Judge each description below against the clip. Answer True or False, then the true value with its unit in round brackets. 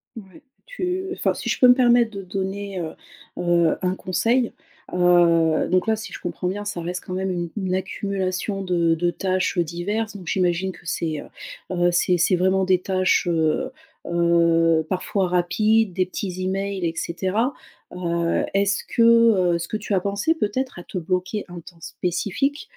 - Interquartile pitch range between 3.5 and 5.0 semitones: False (2.8 semitones)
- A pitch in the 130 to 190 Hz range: True (185 Hz)